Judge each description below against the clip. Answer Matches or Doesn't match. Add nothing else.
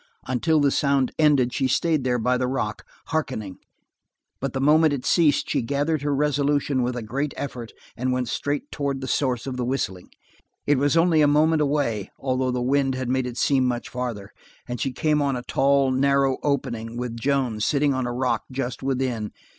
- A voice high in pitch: Doesn't match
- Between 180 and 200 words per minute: Matches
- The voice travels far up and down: Doesn't match